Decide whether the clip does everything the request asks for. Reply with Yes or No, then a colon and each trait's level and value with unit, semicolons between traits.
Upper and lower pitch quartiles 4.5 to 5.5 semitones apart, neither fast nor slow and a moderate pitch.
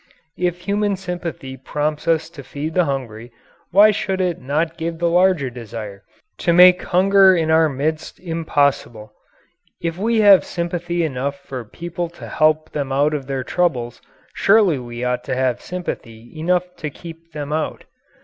Yes: average, 4.8 semitones; average, 160 wpm; medium, 160 Hz